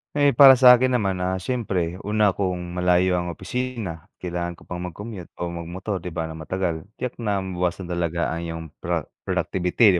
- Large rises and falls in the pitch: No, average, 3.3 semitones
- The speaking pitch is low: Yes, very low, 90 Hz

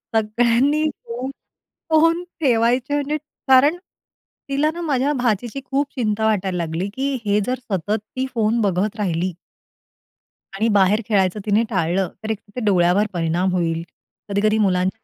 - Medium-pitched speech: No, high, 215 Hz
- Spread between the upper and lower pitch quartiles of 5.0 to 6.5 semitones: Yes, wide, 5.6 semitones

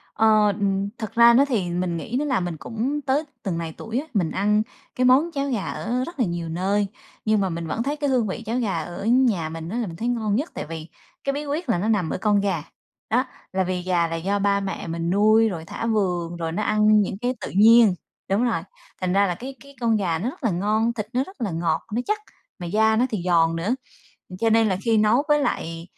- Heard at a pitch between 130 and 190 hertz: No, high, 210 Hz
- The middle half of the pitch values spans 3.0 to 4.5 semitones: No, average, 5.1 semitones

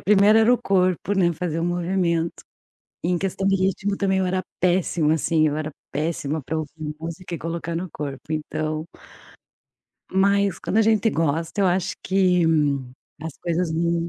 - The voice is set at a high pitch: No, medium, 170 Hz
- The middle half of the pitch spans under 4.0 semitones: Yes, average, 3.1 semitones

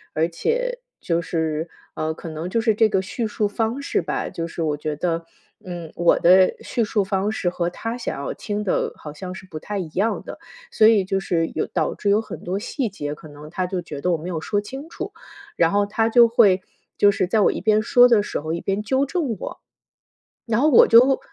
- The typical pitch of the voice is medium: No, high, 195 Hz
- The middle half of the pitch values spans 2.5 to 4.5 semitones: No, average, 4.9 semitones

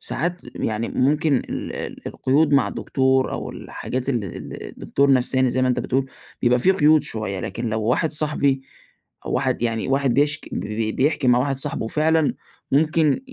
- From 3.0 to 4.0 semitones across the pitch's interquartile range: Yes, average, 3.4 semitones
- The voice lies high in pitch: No, low, 135 Hz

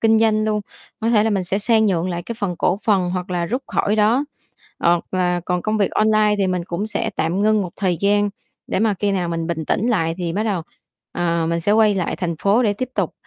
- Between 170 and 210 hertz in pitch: Yes, high, 200 Hz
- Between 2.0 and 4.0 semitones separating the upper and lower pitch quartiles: Yes, average, 3.5 semitones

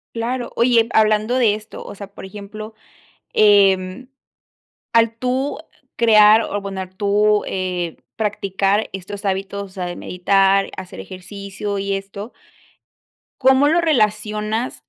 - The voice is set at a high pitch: Yes, high, 205 Hz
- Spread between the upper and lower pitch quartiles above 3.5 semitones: No, narrow, 2.4 semitones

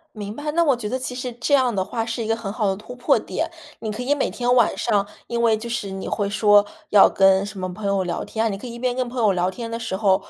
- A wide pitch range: No, average, 3.5 semitones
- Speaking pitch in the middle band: No, high, 220 Hz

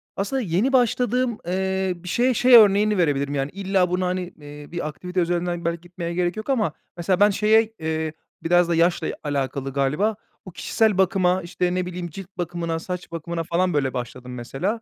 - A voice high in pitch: No, medium, 180 Hz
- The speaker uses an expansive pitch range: No, average, 3.1 semitones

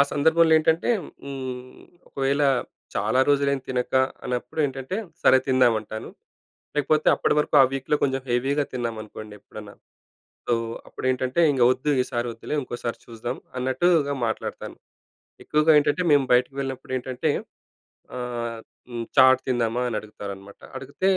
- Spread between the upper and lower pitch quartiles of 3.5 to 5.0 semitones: No, average, 2.7 semitones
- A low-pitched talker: Yes, low, 130 Hz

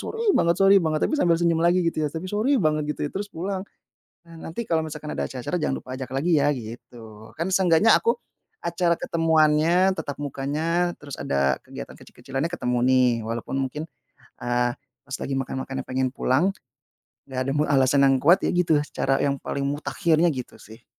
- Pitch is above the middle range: No, medium, 150 Hz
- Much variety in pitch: No, average, 4.3 semitones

